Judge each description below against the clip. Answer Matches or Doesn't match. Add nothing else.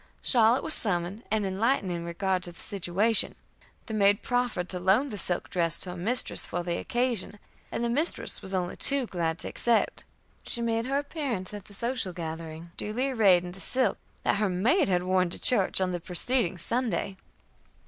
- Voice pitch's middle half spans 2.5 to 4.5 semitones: Doesn't match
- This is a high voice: Matches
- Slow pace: Doesn't match